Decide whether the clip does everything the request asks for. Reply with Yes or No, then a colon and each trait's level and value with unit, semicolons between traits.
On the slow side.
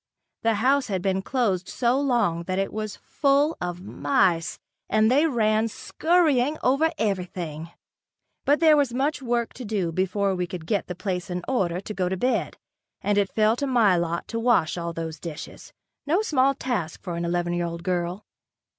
No: average, 185 wpm